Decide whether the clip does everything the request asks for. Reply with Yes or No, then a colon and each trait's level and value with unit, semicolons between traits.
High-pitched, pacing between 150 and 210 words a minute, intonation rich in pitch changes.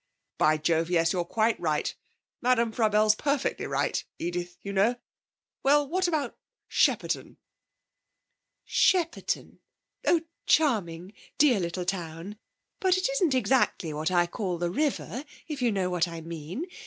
No: high, 205 Hz; slow, 135 wpm; wide, 8.1 semitones